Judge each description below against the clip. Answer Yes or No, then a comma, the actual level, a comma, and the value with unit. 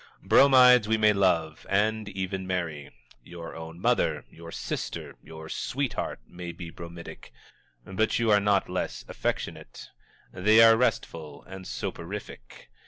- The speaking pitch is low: Yes, very low, 95 Hz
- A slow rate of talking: Yes, slow, 130 wpm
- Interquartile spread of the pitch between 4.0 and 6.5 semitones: Yes, average, 4.5 semitones